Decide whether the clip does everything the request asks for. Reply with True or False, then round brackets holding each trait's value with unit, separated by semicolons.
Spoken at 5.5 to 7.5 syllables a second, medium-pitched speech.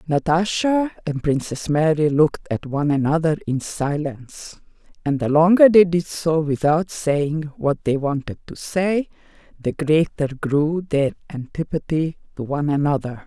False (4.4 syllables/s; 155 Hz)